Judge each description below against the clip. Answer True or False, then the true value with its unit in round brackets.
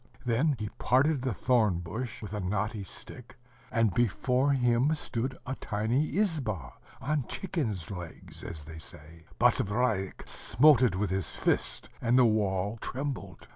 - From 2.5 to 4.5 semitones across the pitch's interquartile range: False (5.1 semitones)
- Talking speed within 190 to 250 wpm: False (145 wpm)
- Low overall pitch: True (115 Hz)